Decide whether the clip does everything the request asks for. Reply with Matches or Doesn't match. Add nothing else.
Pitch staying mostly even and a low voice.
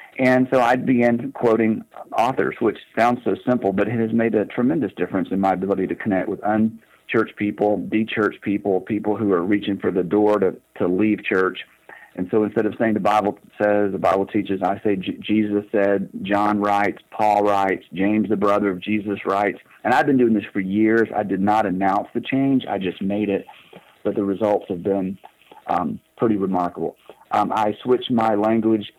Matches